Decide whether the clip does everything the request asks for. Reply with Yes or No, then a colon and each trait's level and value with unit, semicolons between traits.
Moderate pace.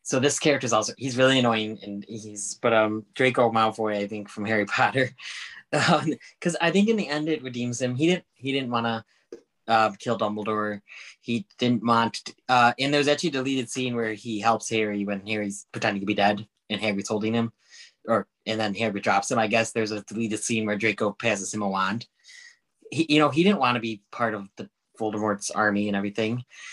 No: fast, 210 wpm